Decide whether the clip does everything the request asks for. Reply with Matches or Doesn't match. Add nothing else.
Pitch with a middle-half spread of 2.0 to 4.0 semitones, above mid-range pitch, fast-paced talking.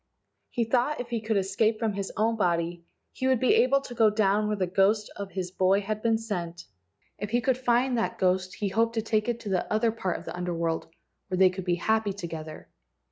Matches